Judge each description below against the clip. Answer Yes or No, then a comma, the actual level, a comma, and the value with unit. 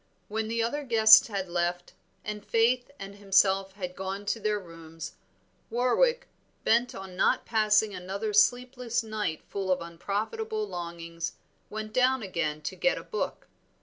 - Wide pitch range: No, average, 4.1 semitones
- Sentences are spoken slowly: No, average, 150 wpm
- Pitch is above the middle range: Yes, high, 210 Hz